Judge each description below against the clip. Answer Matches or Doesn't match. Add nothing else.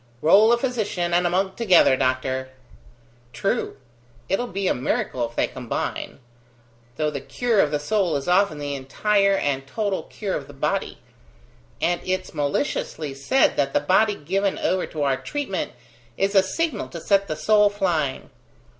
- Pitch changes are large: Matches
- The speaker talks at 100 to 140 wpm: Doesn't match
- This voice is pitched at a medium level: Matches